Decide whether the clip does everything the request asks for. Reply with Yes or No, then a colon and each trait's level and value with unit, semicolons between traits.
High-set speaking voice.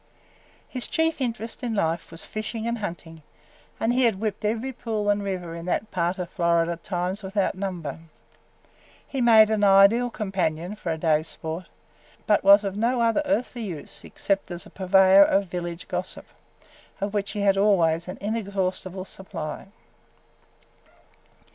Yes: high, 195 Hz